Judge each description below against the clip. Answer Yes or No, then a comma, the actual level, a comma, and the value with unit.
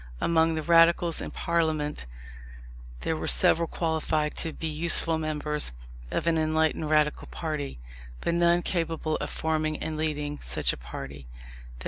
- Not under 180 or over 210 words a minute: No, average, 140 wpm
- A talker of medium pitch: Yes, medium, 160 Hz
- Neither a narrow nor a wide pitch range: No, narrow, 1.5 semitones